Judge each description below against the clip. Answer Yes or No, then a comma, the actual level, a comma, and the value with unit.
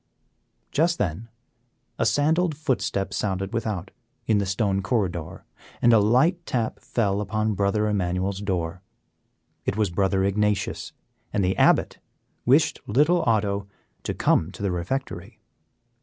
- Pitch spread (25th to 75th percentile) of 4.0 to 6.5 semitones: No, average, 3.6 semitones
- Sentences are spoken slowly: Yes, slow, 130 wpm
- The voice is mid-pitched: No, low, 105 Hz